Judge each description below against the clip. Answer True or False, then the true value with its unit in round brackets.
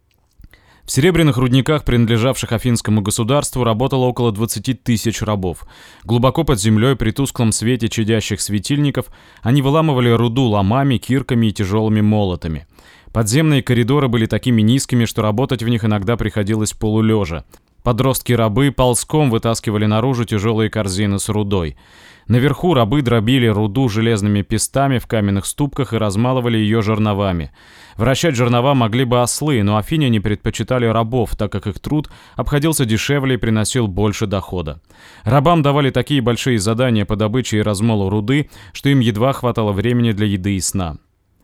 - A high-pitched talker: False (115 Hz)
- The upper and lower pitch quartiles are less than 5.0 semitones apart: True (3.5 semitones)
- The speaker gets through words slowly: False (145 wpm)